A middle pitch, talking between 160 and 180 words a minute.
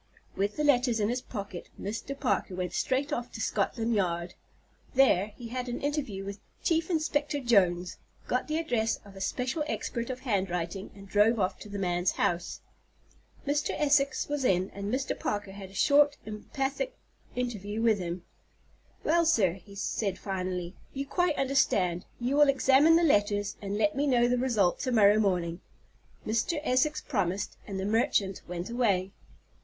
No: high, 220 Hz; average, 170 wpm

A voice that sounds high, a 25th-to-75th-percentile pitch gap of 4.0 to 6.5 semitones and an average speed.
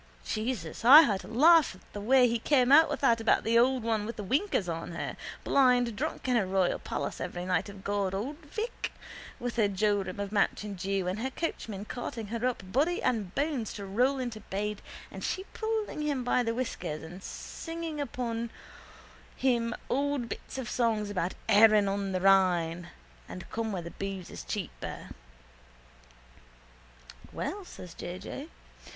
Yes: high, 220 Hz; average, 4.9 semitones; average, 170 wpm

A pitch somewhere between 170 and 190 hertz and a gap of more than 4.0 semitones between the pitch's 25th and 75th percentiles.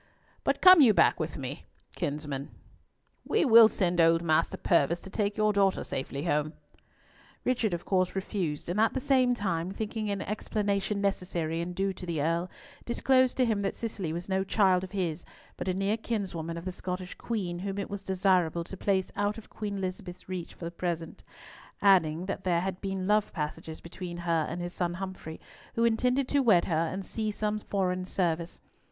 No: medium, 185 Hz; average, 3.3 semitones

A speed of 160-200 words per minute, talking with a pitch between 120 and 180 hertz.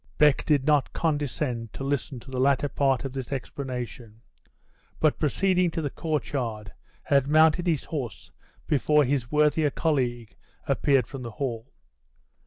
No: average, 150 wpm; medium, 140 Hz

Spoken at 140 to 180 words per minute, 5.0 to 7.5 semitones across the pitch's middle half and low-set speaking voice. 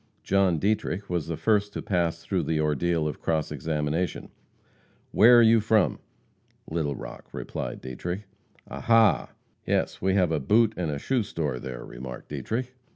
Yes: average, 155 wpm; wide, 5.5 semitones; very low, 85 Hz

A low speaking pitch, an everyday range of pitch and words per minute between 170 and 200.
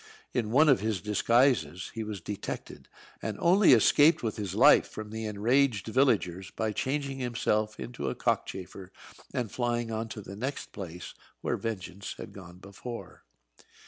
No: low, 110 Hz; average, 3.9 semitones; average, 155 wpm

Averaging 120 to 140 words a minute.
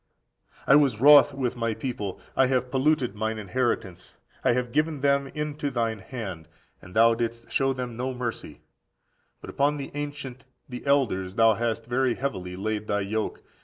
No: average, 170 wpm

